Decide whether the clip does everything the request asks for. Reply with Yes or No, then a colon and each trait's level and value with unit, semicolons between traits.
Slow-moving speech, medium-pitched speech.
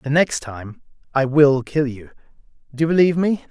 No: average, 190 wpm; medium, 145 Hz